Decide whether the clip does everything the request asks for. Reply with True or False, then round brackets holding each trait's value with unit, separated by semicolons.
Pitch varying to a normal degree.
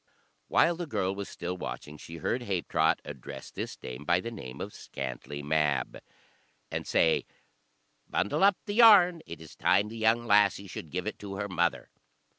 False (6.2 semitones)